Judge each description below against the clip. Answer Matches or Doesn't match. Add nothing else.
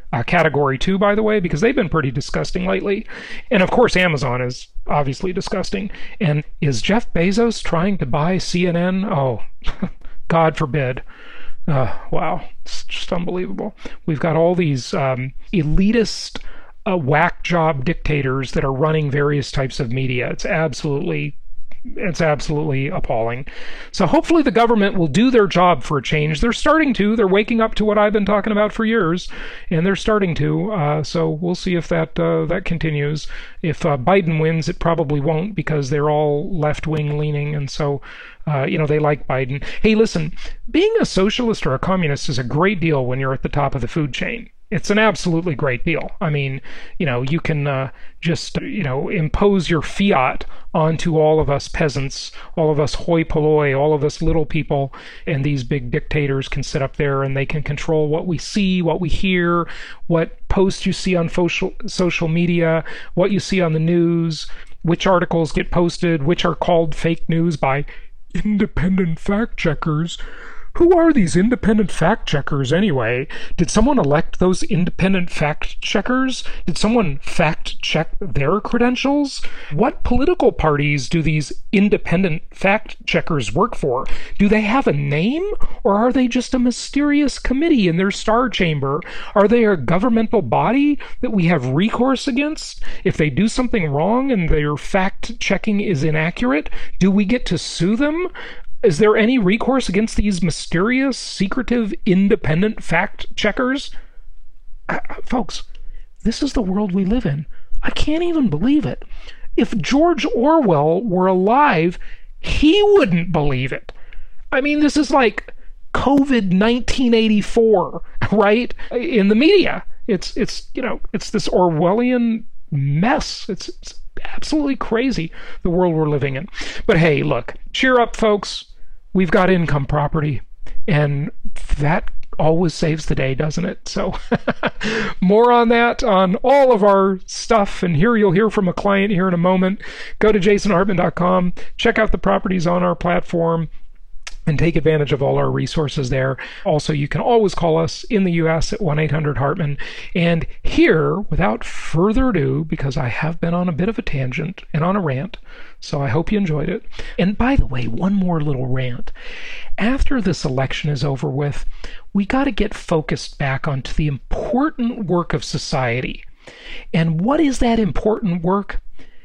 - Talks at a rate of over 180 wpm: Doesn't match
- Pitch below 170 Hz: Doesn't match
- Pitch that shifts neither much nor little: Doesn't match